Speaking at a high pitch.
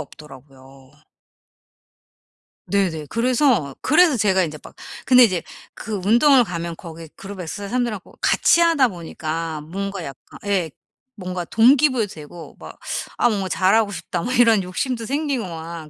Yes: high, 195 Hz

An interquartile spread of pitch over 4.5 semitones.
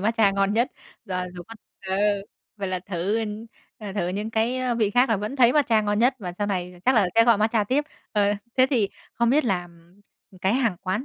No: average, 3.4 semitones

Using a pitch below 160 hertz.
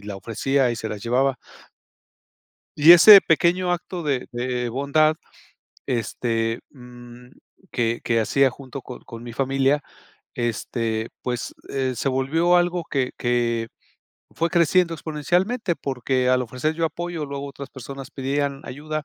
Yes: low, 135 Hz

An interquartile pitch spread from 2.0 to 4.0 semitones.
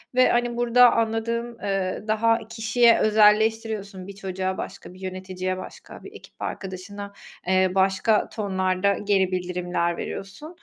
Yes: average, 3.1 semitones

